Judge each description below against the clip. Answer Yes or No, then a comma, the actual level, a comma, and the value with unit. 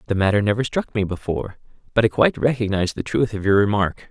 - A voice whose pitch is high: No, low, 105 Hz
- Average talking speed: No, fast, 220 wpm